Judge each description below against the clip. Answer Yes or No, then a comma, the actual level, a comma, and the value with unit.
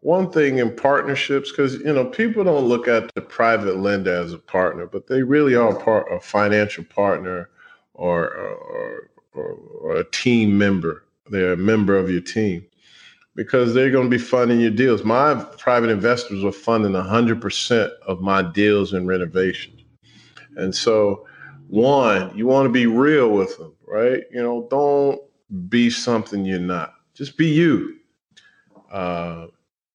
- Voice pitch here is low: Yes, low, 115 Hz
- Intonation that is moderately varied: No, wide, 6.1 semitones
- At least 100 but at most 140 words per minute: No, average, 160 wpm